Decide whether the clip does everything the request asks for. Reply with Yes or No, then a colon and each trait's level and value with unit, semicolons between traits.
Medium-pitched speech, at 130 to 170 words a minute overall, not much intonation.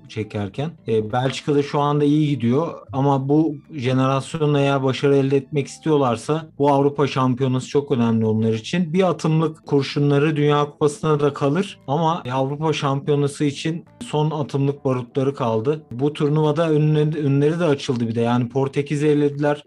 Yes: medium, 145 Hz; fast, 140 wpm; narrow, 2.0 semitones